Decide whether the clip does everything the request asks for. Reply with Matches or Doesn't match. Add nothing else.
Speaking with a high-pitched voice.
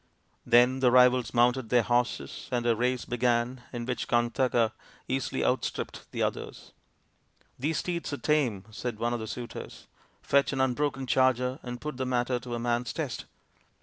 Doesn't match